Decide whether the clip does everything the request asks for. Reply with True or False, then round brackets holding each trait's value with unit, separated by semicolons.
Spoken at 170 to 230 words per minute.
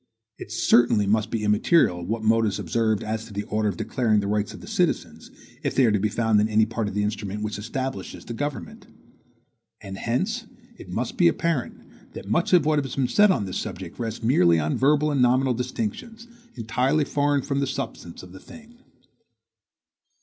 True (200 wpm)